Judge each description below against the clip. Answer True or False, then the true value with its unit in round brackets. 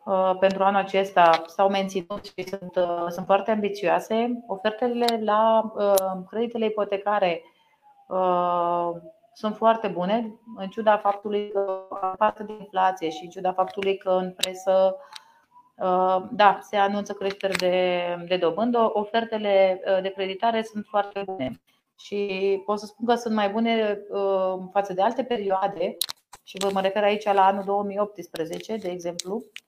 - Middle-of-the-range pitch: False (200 Hz)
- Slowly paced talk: False (150 wpm)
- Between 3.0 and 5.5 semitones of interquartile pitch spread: False (2.4 semitones)